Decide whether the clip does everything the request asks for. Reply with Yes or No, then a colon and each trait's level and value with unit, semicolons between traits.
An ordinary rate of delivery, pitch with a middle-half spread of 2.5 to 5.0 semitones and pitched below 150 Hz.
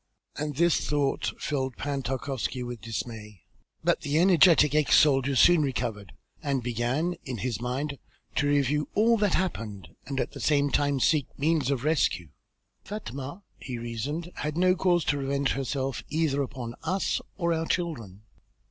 Yes: average, 155 wpm; average, 4.1 semitones; medium, 140 Hz